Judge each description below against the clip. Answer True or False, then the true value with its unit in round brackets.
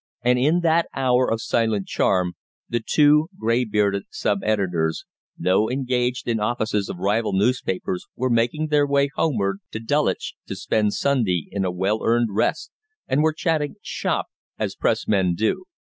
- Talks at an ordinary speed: True (160 wpm)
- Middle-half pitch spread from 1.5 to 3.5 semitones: False (5.5 semitones)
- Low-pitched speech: True (115 Hz)